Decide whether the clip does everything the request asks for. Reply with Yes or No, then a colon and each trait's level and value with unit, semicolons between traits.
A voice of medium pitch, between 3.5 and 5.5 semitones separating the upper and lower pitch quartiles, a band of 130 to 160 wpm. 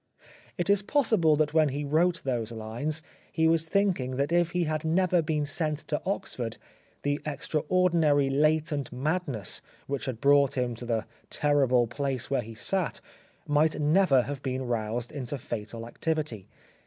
Yes: medium, 145 Hz; average, 4.3 semitones; average, 155 wpm